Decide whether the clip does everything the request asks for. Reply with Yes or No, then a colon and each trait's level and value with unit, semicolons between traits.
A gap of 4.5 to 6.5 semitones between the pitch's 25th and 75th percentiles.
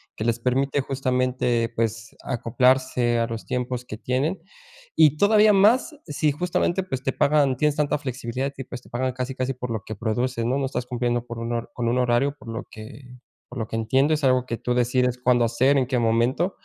No: narrow, 2.6 semitones